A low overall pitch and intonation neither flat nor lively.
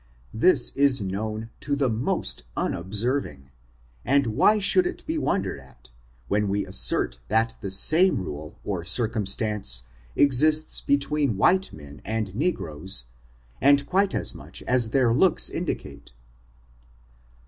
No: low, 110 Hz; wide, 6.8 semitones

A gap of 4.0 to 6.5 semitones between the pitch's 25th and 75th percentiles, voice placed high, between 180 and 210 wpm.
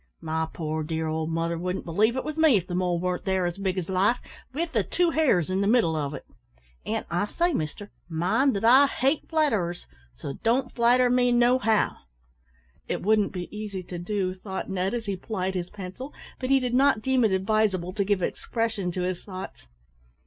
Yes: average, 5.2 semitones; high, 195 Hz; fast, 205 wpm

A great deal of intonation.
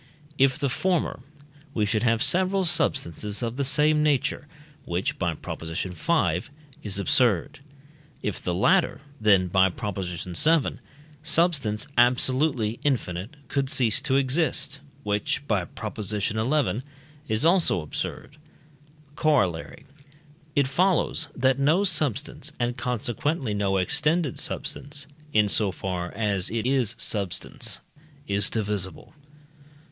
Yes: wide, 6.5 semitones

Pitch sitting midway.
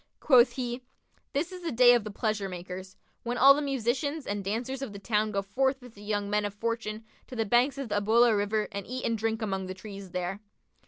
No: high, 220 Hz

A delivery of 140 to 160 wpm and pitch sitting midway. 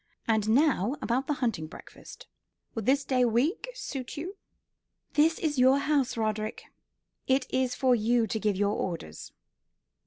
No: average, 150 wpm; very high, 250 Hz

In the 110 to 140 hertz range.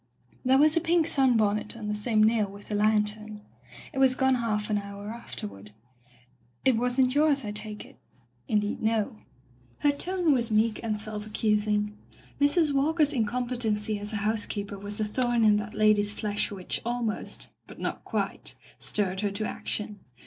No: high, 215 Hz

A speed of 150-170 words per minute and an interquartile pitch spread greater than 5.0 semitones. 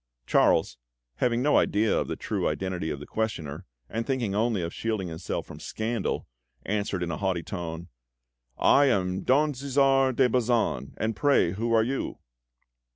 Yes: average, 160 wpm; wide, 5.5 semitones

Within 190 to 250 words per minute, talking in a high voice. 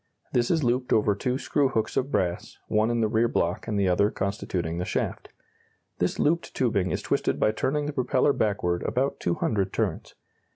No: average, 195 wpm; low, 110 Hz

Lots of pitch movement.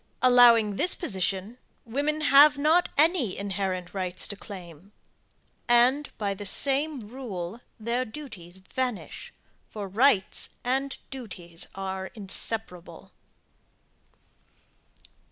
Yes: wide, 5.9 semitones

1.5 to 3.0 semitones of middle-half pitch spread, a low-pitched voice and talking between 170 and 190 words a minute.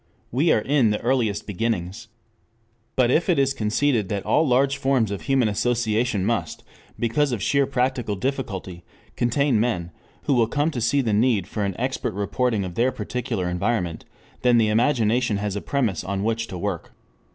No: average, 4.0 semitones; low, 115 Hz; average, 175 wpm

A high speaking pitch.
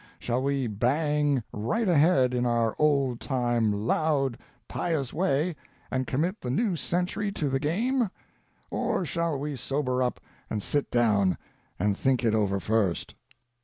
No: low, 135 Hz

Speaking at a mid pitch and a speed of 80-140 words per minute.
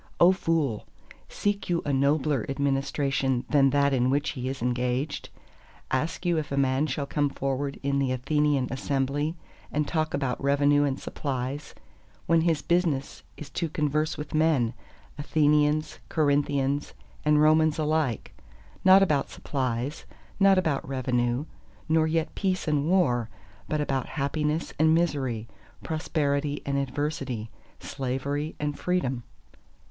Yes: medium, 145 Hz; slow, 135 wpm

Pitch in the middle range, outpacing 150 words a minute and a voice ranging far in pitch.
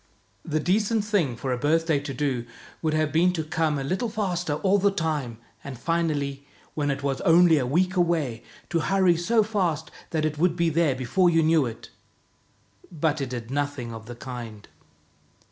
No: medium, 155 Hz; average, 185 wpm; average, 4.2 semitones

